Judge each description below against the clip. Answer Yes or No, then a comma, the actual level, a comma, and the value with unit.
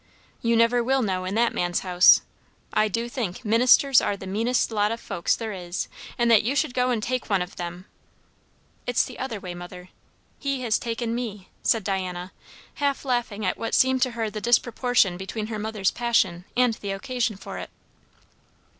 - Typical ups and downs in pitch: Yes, average, 4.2 semitones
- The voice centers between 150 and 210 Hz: No, high, 220 Hz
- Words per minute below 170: No, average, 190 wpm